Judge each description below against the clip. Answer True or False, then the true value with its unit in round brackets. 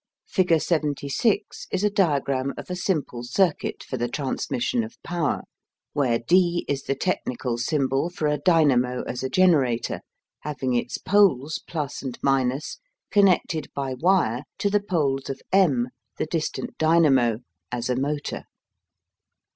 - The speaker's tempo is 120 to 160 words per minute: True (140 wpm)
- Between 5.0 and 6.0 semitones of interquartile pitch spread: True (5.5 semitones)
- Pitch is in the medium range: True (145 Hz)